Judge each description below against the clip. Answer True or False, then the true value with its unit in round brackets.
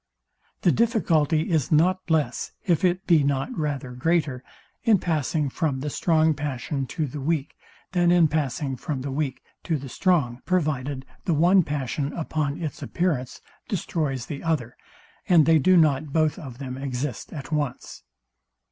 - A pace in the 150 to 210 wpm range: True (155 wpm)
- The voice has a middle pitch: True (150 Hz)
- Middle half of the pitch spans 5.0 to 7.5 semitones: False (3.5 semitones)